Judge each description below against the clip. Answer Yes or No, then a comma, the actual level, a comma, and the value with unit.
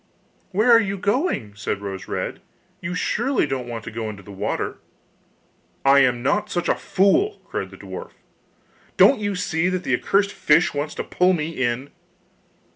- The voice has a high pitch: No, medium, 165 Hz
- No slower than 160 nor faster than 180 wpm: Yes, average, 175 wpm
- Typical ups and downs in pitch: No, wide, 8.7 semitones